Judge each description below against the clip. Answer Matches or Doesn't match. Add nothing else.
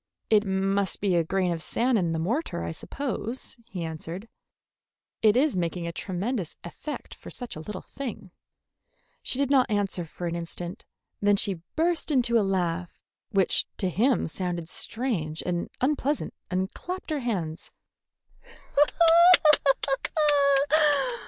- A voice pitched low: Doesn't match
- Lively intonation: Matches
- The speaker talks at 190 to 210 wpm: Doesn't match